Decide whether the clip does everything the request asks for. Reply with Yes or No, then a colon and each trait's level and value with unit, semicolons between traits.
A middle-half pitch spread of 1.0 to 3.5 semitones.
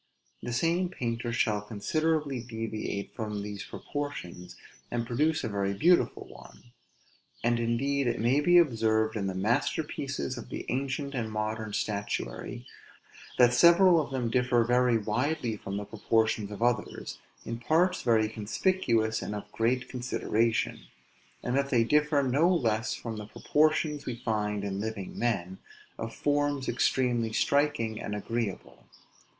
No: average, 4.3 semitones